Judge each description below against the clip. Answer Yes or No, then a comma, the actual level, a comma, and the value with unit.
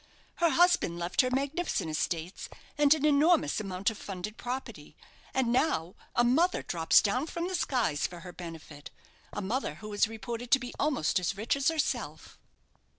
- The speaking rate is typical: Yes, average, 170 wpm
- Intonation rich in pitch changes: Yes, wide, 7.6 semitones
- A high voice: Yes, high, 235 Hz